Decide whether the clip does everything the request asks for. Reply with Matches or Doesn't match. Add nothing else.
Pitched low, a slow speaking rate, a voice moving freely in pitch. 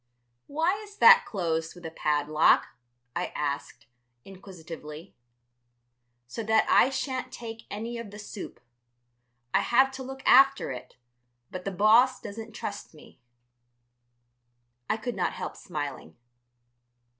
Doesn't match